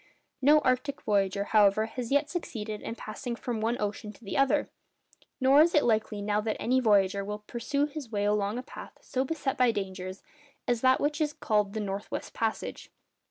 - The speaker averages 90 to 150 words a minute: No, average, 195 wpm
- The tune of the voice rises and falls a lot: No, average, 4.2 semitones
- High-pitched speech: Yes, high, 225 Hz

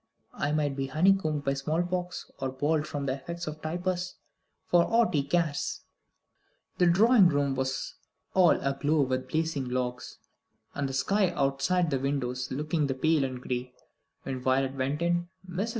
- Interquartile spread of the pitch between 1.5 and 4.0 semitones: No, average, 4.4 semitones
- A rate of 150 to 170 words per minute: Yes, average, 165 wpm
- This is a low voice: No, medium, 145 Hz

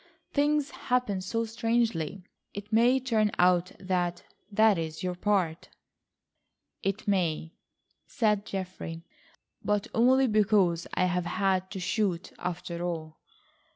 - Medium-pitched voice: No, high, 195 Hz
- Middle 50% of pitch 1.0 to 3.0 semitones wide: No, average, 3.8 semitones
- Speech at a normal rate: No, slow, 120 wpm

